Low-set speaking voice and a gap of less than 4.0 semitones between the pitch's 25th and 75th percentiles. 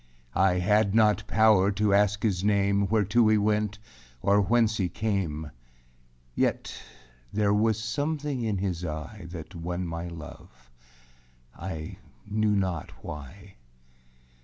Yes: low, 100 Hz; average, 3.3 semitones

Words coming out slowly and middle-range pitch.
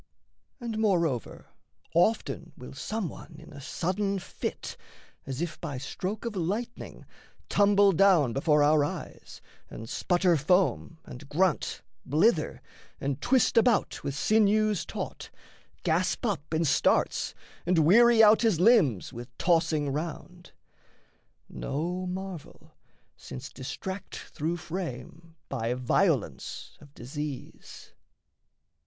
Yes: slow, 115 wpm; medium, 170 Hz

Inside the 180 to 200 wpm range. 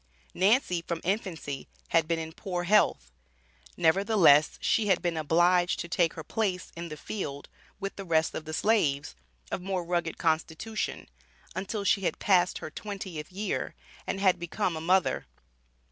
No: average, 160 wpm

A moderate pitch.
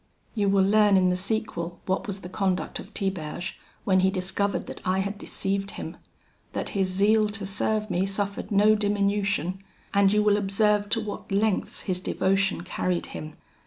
No: high, 195 Hz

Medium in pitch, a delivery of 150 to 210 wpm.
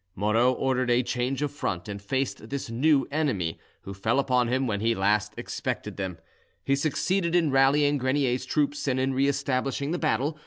No: low, 130 Hz; average, 185 wpm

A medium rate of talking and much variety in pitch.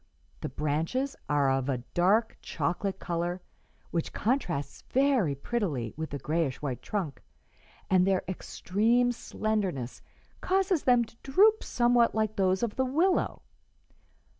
No: slow, 130 wpm; wide, 8.0 semitones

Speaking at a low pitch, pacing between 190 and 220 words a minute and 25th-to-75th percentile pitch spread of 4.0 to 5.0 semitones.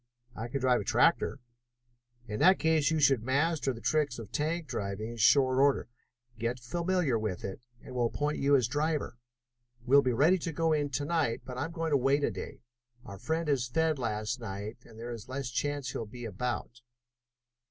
Yes: low, 130 Hz; average, 200 wpm; average, 4.3 semitones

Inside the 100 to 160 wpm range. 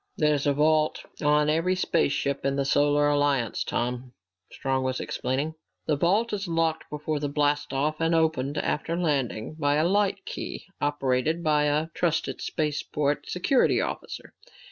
Yes: average, 155 wpm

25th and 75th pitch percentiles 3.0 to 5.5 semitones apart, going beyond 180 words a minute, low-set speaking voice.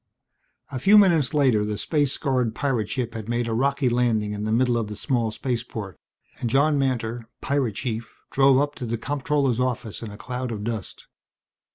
Yes: average, 3.4 semitones; average, 190 wpm; low, 120 Hz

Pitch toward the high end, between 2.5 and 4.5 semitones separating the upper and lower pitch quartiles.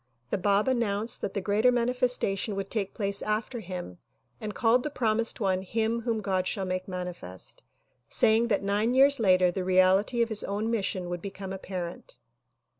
Yes: high, 205 Hz; average, 3.5 semitones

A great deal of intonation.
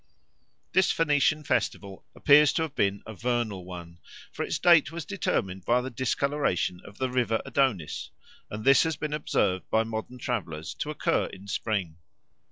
Yes: wide, 6.8 semitones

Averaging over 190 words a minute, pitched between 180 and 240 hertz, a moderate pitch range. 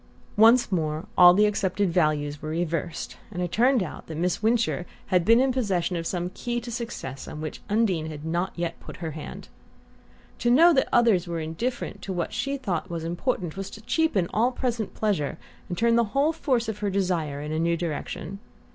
No: average, 200 wpm; medium, 185 Hz; wide, 5.7 semitones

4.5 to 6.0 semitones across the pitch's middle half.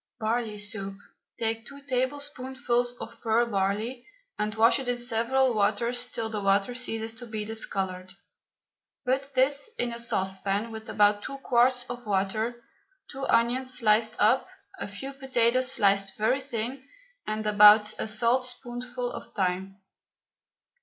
No: average, 3.1 semitones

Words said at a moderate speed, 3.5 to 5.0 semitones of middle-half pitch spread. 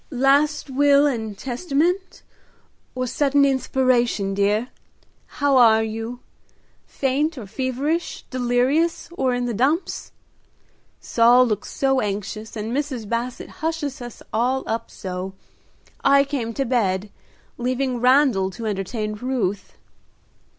No: slow, 115 wpm; average, 4.0 semitones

